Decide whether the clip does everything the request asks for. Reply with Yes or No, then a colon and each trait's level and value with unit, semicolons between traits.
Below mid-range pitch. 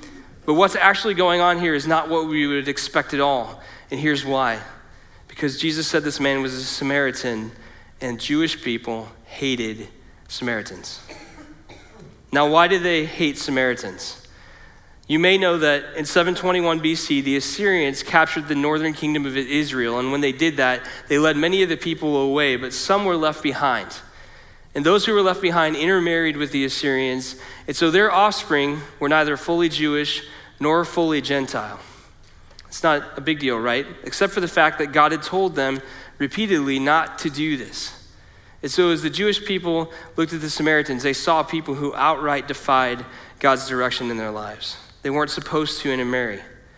No: medium, 145 Hz